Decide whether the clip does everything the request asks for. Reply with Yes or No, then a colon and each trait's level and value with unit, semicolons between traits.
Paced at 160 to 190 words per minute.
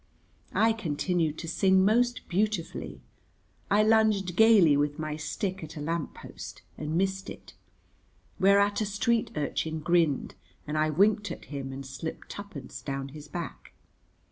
No: average, 145 wpm